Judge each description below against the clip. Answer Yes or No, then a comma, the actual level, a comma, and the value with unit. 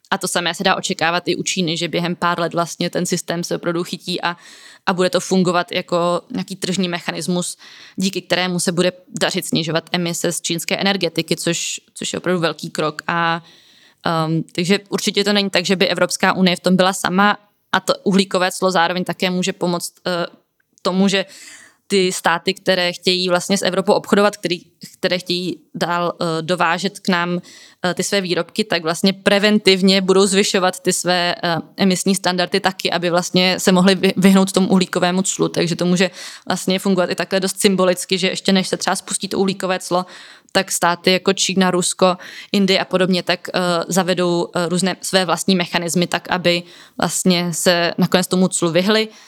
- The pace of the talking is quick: Yes, fast, 180 wpm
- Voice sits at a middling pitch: Yes, medium, 180 Hz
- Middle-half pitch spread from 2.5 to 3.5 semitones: No, narrow, 1.5 semitones